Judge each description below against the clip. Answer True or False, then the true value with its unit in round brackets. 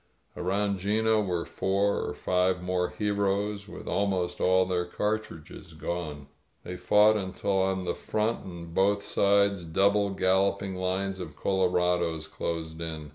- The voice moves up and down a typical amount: False (2.3 semitones)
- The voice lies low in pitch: True (95 Hz)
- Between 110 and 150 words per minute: True (140 wpm)